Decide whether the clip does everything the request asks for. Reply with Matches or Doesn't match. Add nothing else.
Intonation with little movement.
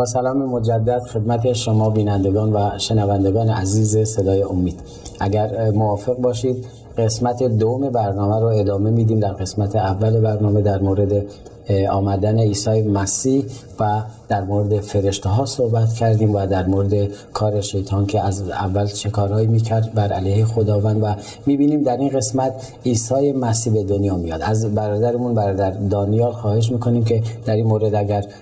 Matches